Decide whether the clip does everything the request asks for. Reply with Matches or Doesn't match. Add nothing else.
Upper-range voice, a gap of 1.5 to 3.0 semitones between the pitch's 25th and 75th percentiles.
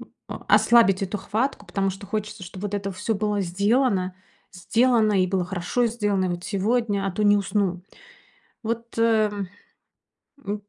Matches